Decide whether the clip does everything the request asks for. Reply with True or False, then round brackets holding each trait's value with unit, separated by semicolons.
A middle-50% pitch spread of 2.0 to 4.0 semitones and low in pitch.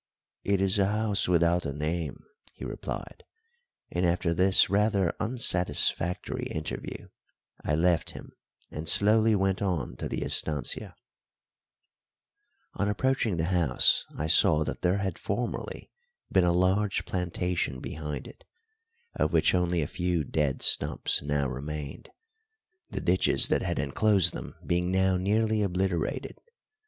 True (3.7 semitones; 90 Hz)